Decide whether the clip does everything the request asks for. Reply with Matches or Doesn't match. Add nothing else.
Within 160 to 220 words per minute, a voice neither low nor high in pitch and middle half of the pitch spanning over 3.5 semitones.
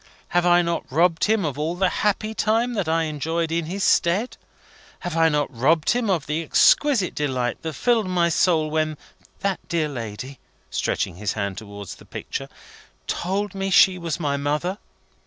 Matches